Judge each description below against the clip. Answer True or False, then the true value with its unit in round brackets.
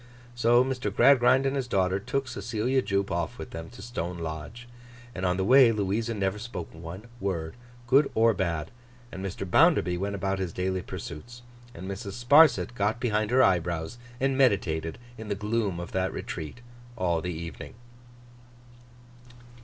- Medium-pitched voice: False (100 Hz)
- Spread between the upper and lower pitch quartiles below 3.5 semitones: False (5.1 semitones)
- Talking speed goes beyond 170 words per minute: False (160 wpm)